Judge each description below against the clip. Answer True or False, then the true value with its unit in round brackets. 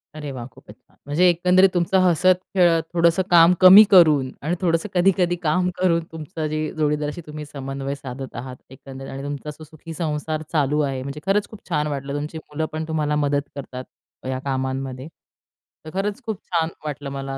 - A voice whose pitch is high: False (155 Hz)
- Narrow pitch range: False (3.8 semitones)